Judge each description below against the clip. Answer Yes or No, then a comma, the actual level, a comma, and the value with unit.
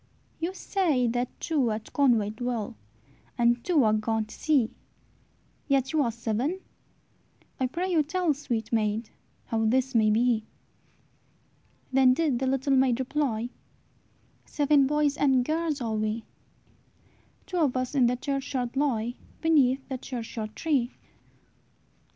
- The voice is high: Yes, very high, 255 Hz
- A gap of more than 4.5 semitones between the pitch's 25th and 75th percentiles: No, average, 4.0 semitones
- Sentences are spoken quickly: No, slow, 135 wpm